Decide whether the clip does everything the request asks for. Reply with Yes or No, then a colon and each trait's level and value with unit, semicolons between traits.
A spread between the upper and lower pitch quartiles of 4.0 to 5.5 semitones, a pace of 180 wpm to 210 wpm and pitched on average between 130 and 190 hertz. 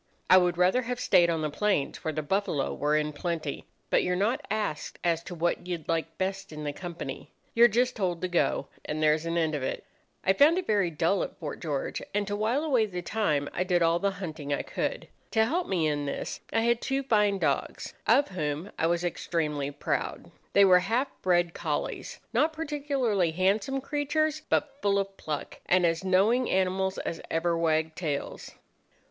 Yes: average, 5.1 semitones; average, 200 wpm; medium, 185 Hz